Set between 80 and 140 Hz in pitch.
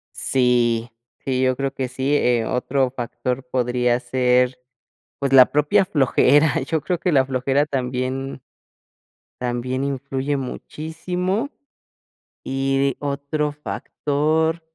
Yes: low, 135 Hz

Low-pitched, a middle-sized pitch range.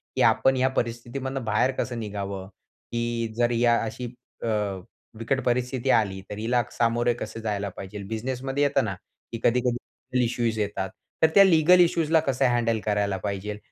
Yes: low, 120 Hz; average, 3.4 semitones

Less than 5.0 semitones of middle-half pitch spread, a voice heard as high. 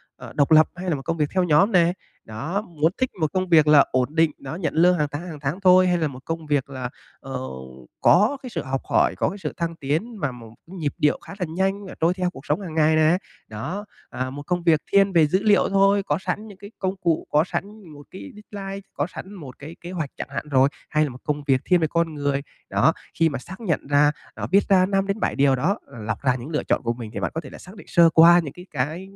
No: average, 4.5 semitones; medium, 165 Hz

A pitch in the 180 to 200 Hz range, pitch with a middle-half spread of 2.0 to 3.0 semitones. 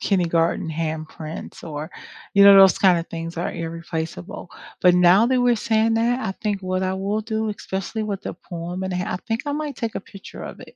No: high, 190 Hz; average, 4.5 semitones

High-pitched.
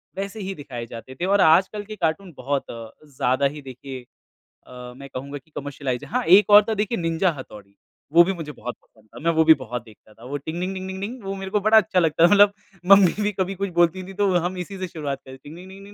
No: medium, 170 Hz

